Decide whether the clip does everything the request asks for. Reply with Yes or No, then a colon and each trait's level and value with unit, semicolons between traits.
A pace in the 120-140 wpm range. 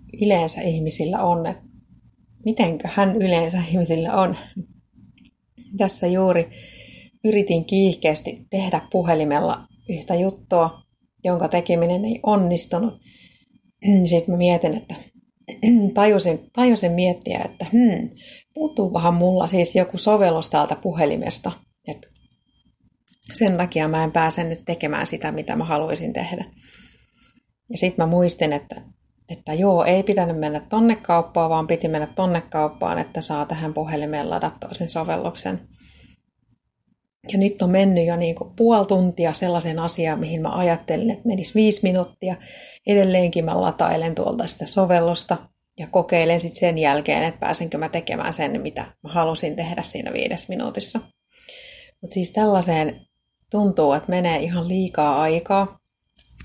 Yes: average, 130 wpm